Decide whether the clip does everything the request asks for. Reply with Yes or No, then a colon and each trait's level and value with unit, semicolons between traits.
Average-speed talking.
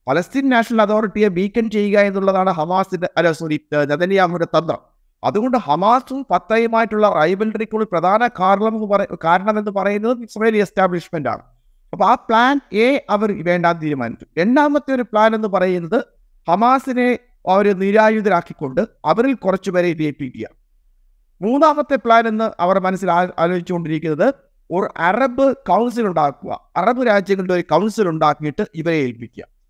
Yes: average, 115 wpm